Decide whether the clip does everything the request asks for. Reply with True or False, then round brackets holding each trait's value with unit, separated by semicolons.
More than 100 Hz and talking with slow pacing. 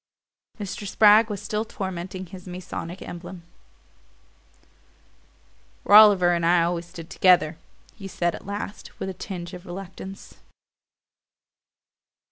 True (185 Hz; 110 wpm)